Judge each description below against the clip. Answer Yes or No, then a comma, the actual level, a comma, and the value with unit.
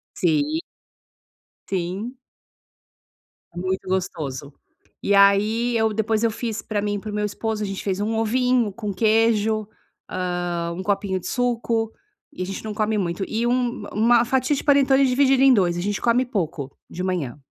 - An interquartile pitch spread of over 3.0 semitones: Yes, average, 4.0 semitones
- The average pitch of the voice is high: Yes, high, 215 Hz